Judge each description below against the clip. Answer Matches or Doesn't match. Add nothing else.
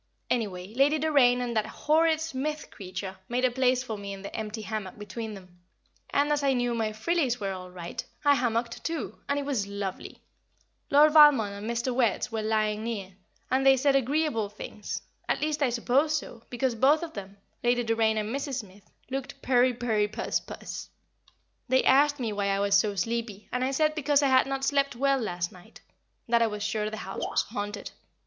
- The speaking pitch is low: Doesn't match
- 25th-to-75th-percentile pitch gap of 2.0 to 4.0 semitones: Doesn't match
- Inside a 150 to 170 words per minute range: Doesn't match